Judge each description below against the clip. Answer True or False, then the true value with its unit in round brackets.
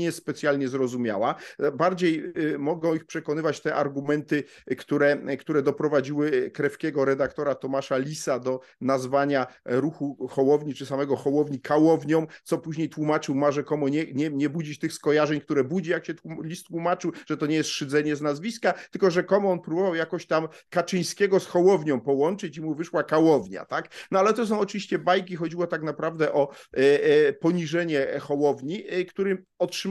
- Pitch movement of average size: True (3.4 semitones)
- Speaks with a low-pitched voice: False (155 Hz)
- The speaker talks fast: True (165 wpm)